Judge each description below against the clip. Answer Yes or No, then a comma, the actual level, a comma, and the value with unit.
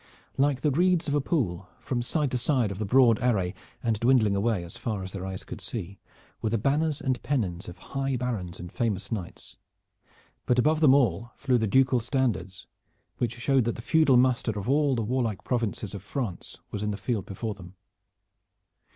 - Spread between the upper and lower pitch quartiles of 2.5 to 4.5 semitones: No, average, 4.9 semitones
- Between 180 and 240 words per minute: Yes, average, 195 wpm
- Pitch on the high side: No, low, 120 Hz